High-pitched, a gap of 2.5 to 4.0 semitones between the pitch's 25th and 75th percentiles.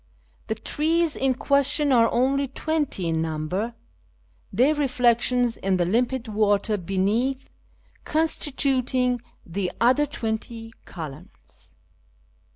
No: high, 240 Hz; average, 5.1 semitones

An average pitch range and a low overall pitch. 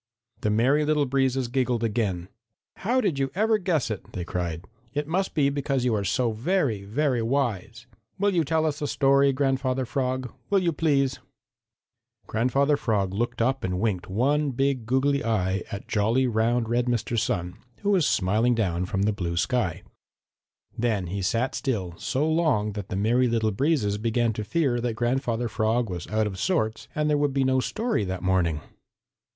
Yes: average, 4.8 semitones; low, 120 Hz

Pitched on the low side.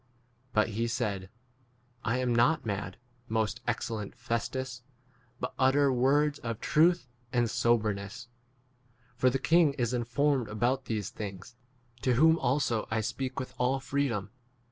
Yes: low, 120 Hz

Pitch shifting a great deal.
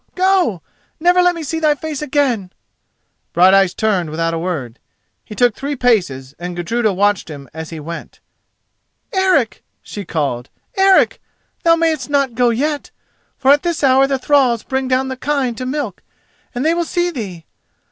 Yes: wide, 8.5 semitones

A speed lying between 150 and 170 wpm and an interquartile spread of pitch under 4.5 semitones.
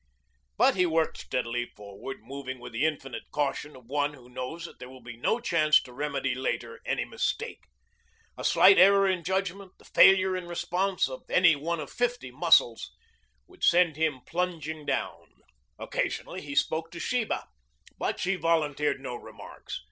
No: average, 165 wpm; wide, 5.4 semitones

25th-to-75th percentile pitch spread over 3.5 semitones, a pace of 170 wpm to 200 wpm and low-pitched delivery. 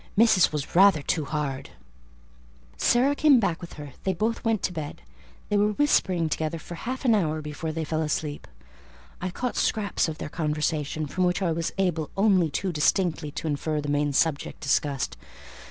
No: average, 4.5 semitones; average, 180 wpm; medium, 165 Hz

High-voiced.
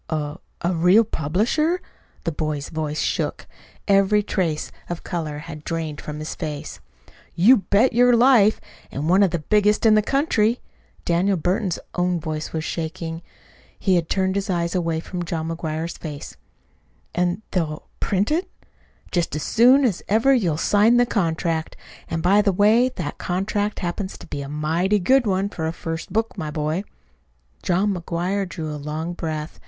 No: medium, 175 Hz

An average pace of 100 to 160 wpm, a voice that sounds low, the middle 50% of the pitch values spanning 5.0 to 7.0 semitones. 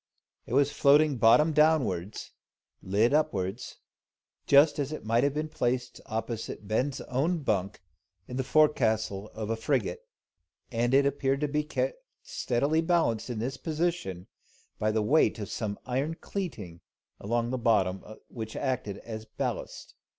Yes: average, 150 wpm; low, 125 Hz; wide, 5.4 semitones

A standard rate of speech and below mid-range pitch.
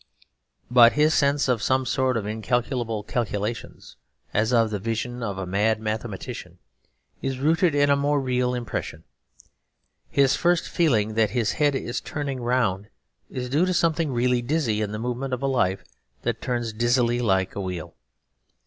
Yes: average, 165 wpm; low, 120 Hz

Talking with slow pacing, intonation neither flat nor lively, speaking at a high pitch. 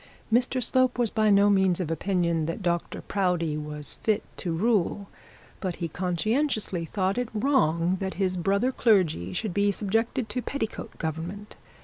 No: average, 160 wpm; average, 4.3 semitones; high, 195 Hz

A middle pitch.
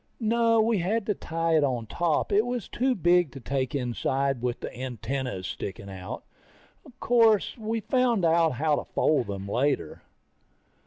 Yes: medium, 155 Hz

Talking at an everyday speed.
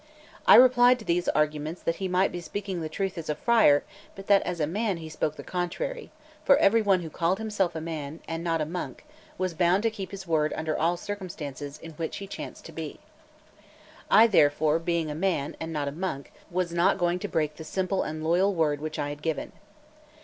No: fast, 220 wpm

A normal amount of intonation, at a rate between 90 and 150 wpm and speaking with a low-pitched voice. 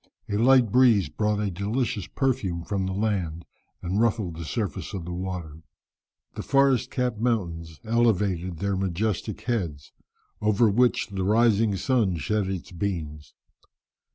Yes: average, 4.5 semitones; average, 140 wpm; low, 100 Hz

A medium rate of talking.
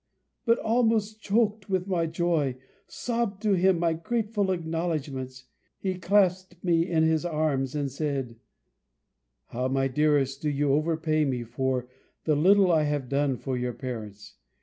Yes: average, 150 wpm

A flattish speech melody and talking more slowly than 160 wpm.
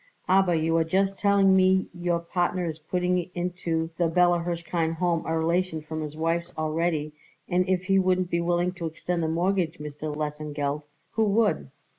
No: narrow, 2.2 semitones; average, 175 wpm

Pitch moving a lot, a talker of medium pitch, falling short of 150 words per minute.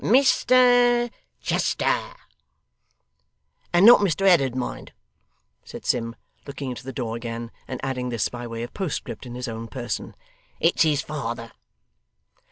No: wide, 8.3 semitones; low, 130 Hz; slow, 135 wpm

